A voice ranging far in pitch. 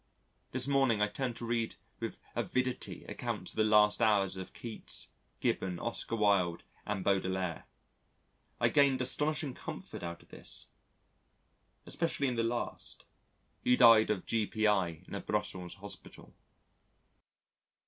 No: average, 4.3 semitones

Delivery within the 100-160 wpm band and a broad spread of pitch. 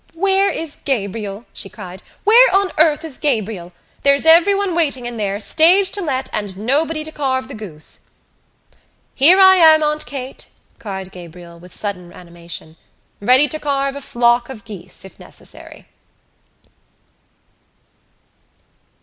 Yes: slow, 135 wpm; wide, 8.0 semitones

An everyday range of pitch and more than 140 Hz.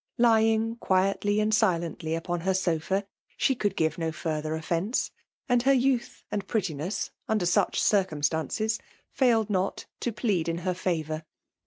Yes: average, 5.0 semitones; high, 190 Hz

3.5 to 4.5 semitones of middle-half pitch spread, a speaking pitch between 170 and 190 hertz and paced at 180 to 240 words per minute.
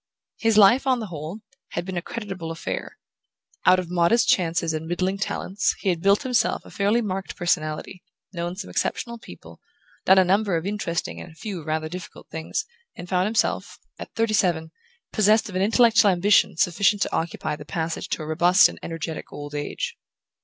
Yes: average, 3.8 semitones; medium, 185 Hz; average, 185 wpm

